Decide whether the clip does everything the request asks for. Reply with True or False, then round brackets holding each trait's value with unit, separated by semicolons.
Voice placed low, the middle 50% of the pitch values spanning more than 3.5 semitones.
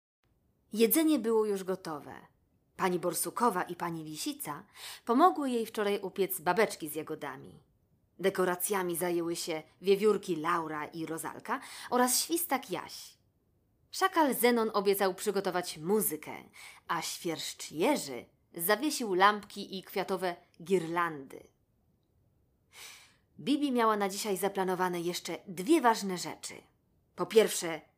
False (190 Hz; 4.1 semitones)